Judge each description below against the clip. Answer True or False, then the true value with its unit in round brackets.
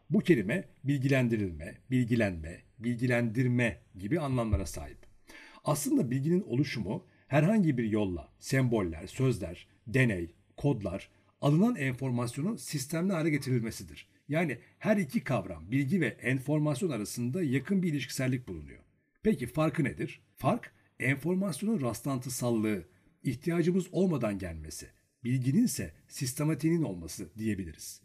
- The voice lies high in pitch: False (125 Hz)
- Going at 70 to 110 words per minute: True (105 wpm)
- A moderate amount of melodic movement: False (7.1 semitones)